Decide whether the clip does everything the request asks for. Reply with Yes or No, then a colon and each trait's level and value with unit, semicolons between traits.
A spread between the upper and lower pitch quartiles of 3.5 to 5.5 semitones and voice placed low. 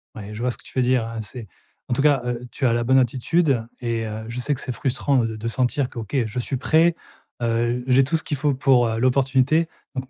No: average, 2.7 semitones; low, 125 Hz